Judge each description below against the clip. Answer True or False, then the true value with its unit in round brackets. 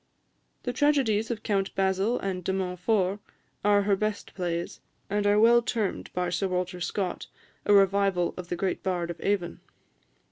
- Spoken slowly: False (165 wpm)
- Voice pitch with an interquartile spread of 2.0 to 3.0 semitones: True (2.4 semitones)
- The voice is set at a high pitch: True (195 Hz)